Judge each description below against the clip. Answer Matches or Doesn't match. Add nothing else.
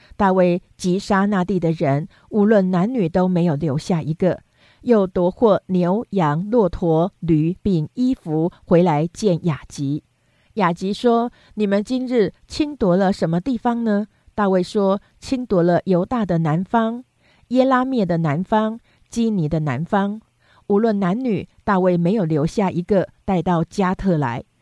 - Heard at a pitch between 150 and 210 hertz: Matches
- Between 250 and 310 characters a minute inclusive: Doesn't match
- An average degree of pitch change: Matches